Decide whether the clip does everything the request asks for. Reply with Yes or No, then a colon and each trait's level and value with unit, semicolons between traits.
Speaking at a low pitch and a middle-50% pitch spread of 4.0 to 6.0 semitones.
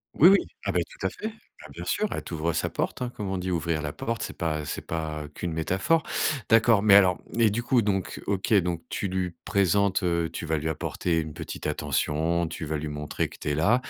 Yes: very low, 90 Hz; average, 4.3 semitones